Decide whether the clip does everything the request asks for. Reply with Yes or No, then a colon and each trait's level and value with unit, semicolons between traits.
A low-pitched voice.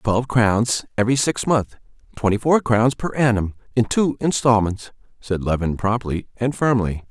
Yes: low, 115 Hz